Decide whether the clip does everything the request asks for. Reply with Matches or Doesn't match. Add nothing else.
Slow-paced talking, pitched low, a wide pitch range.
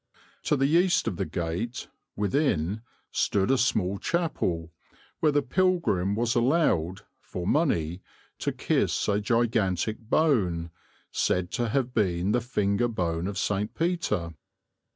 Matches